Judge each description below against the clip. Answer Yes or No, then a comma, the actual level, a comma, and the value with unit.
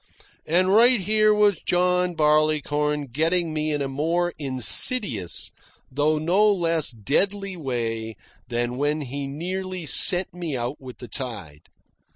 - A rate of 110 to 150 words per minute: Yes, slow, 135 wpm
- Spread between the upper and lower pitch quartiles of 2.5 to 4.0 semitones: No, average, 5.2 semitones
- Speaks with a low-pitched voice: No, medium, 155 Hz